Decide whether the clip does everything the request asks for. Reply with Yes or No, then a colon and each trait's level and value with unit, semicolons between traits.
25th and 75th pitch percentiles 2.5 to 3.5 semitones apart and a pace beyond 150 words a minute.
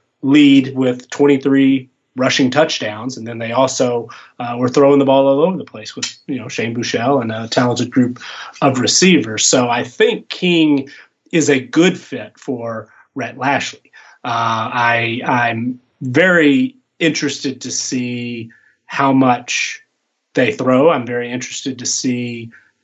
No: average, 2.8 semitones; average, 145 wpm